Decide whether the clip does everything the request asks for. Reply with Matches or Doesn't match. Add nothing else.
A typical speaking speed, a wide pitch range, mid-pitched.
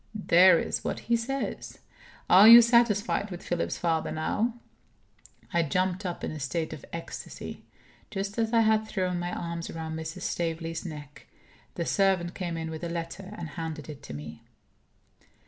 Doesn't match